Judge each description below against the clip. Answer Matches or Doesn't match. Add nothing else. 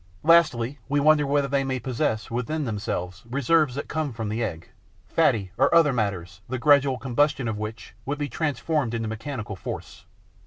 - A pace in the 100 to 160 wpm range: Doesn't match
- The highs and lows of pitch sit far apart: Doesn't match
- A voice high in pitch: Doesn't match